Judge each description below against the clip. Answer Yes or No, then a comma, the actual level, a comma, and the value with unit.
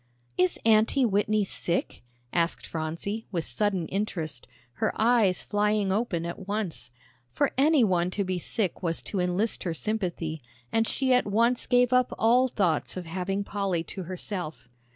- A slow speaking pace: No, average, 155 wpm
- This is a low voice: No, high, 195 Hz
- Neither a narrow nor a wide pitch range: Yes, average, 4.2 semitones